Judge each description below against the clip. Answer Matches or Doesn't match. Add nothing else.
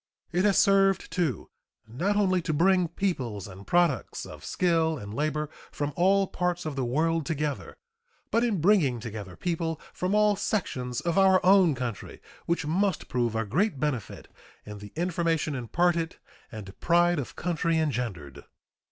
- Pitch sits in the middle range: Matches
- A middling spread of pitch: Doesn't match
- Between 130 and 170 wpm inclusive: Matches